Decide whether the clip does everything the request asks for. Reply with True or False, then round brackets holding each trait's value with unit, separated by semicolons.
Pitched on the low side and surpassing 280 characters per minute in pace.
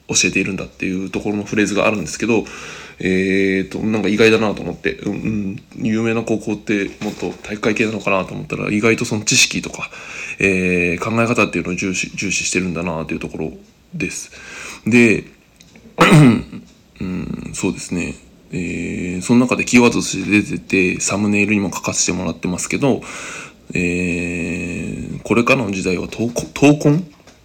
True (100 Hz; 350 characters per minute)